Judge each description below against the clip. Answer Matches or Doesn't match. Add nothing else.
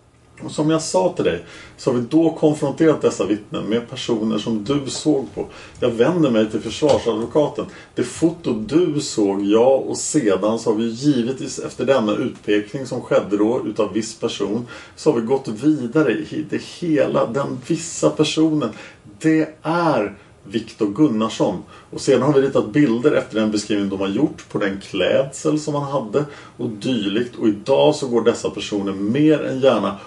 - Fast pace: Doesn't match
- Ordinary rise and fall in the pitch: Doesn't match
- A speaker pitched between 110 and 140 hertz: Matches